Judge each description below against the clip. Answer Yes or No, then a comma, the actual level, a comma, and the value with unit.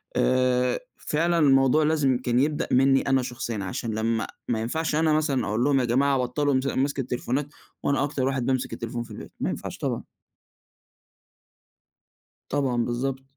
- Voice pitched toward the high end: No, low, 130 Hz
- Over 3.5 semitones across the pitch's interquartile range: No, narrow, 2.5 semitones